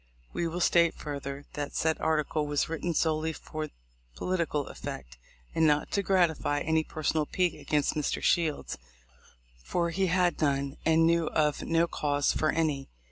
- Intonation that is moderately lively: No, narrow, 2.3 semitones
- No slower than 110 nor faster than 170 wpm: Yes, average, 155 wpm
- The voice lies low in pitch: No, medium, 155 Hz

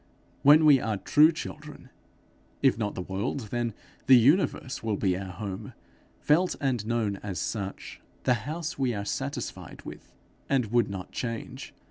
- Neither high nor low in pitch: No, low, 115 Hz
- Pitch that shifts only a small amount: No, wide, 5.4 semitones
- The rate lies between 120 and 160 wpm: Yes, average, 155 wpm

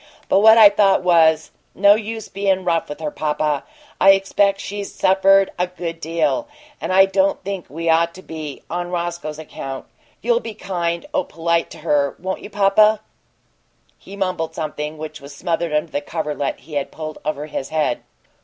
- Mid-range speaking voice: Yes, medium, 170 Hz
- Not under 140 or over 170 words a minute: No, average, 180 wpm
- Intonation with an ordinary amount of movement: Yes, average, 4.0 semitones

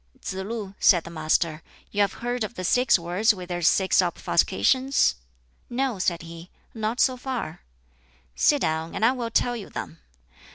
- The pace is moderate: Yes, average, 170 wpm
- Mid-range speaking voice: No, high, 200 Hz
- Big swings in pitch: Yes, wide, 6.0 semitones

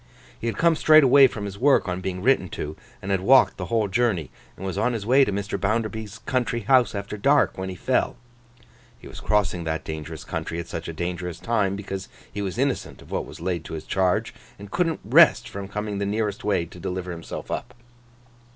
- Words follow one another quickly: Yes, fast, 215 wpm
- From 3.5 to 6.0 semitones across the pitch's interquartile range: Yes, average, 4.3 semitones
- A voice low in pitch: Yes, low, 100 Hz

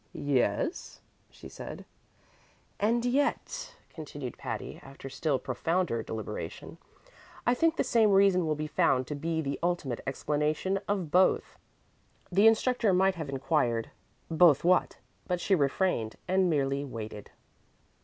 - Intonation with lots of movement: Yes, wide, 5.8 semitones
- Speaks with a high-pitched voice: No, medium, 160 Hz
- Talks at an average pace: No, slow, 130 wpm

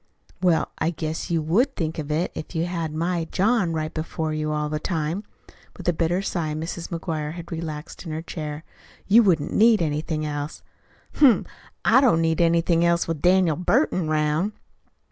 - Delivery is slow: No, average, 180 wpm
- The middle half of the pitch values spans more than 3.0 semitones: No, narrow, 2.4 semitones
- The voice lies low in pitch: No, medium, 165 Hz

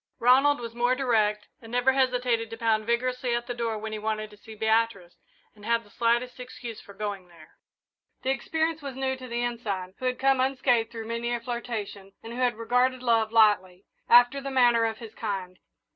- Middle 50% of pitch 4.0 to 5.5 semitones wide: No, narrow, 2.6 semitones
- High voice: Yes, high, 235 Hz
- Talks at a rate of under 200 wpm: No, fast, 205 wpm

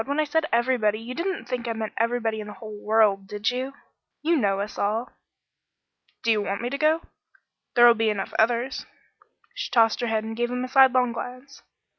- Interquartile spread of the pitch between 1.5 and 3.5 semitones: Yes, average, 2.8 semitones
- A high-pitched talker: Yes, high, 235 Hz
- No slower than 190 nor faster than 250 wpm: Yes, fast, 205 wpm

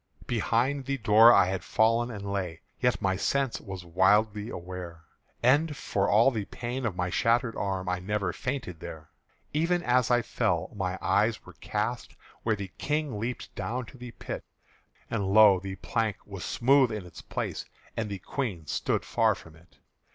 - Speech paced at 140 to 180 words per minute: Yes, average, 175 wpm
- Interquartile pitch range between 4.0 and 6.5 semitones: Yes, average, 4.5 semitones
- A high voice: No, low, 105 Hz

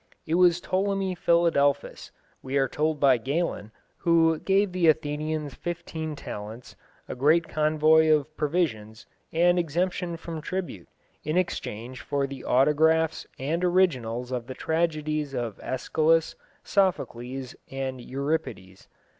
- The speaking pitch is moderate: Yes, medium, 155 Hz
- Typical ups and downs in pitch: Yes, average, 4.1 semitones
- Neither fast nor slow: No, slow, 120 wpm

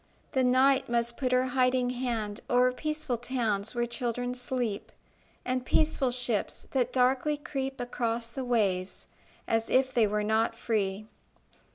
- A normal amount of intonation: No, narrow, 2.1 semitones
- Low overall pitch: No, high, 245 Hz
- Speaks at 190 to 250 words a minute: No, average, 145 wpm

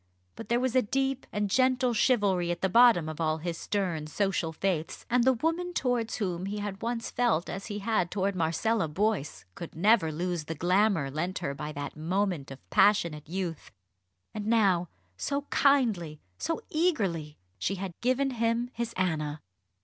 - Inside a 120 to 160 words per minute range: No, average, 170 wpm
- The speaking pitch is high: Yes, high, 195 Hz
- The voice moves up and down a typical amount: No, wide, 6.0 semitones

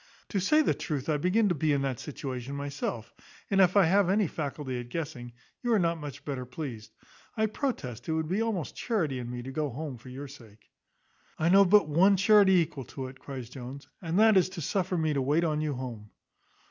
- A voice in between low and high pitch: Yes, medium, 150 Hz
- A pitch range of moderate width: No, wide, 6.1 semitones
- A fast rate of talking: Yes, fast, 225 wpm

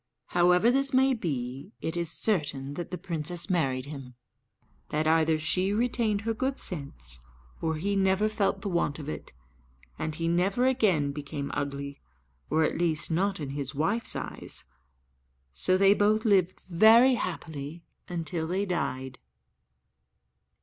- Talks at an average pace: Yes, average, 145 wpm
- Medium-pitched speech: Yes, medium, 170 Hz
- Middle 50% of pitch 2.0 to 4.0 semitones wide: No, wide, 5.5 semitones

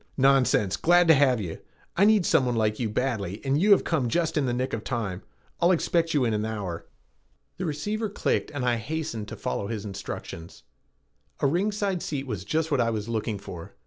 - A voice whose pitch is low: Yes, low, 130 Hz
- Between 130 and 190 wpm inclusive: No, fast, 205 wpm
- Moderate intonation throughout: No, wide, 7.2 semitones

